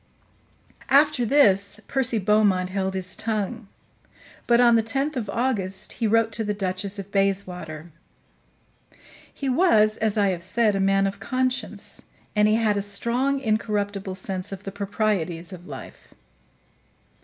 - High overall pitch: Yes, high, 205 Hz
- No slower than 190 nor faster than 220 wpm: No, average, 145 wpm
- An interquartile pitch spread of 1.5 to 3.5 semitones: Yes, average, 3.0 semitones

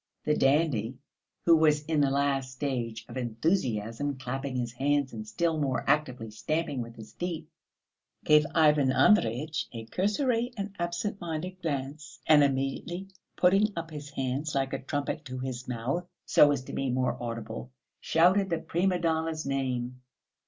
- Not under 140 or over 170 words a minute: Yes, average, 155 wpm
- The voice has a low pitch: No, medium, 145 Hz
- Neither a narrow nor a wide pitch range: Yes, average, 4.3 semitones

